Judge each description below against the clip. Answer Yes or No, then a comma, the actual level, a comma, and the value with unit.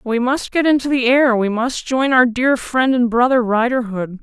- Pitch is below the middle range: No, high, 245 Hz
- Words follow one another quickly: Yes, fast, 215 wpm